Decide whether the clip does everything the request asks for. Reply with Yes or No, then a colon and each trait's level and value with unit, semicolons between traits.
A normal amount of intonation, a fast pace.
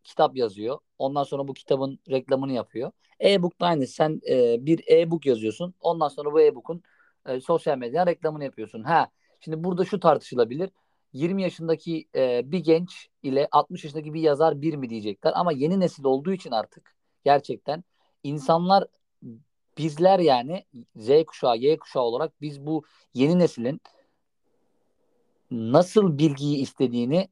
Yes: average, 4.3 semitones; fast, 145 wpm